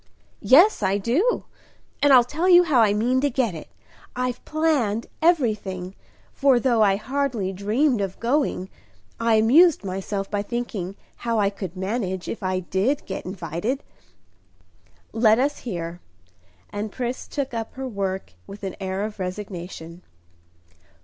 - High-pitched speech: Yes, high, 215 Hz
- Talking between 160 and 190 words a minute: No, average, 145 wpm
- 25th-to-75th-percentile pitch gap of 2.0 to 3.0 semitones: No, average, 5.2 semitones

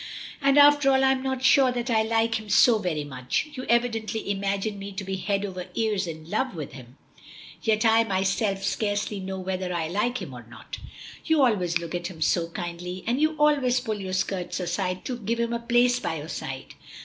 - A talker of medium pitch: No, high, 205 Hz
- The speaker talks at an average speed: No, fast, 210 wpm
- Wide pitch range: No, average, 5.0 semitones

